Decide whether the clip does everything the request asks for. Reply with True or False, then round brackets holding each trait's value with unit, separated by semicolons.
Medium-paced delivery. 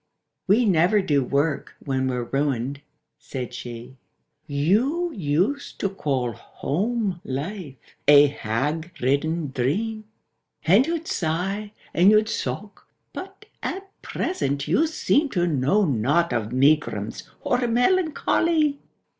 False (120 wpm)